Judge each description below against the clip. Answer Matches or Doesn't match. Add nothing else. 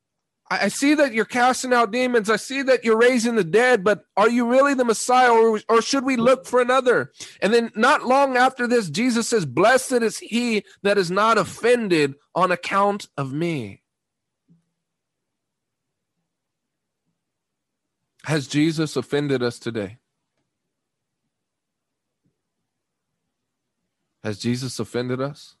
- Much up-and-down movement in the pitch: Matches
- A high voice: Matches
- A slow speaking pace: Matches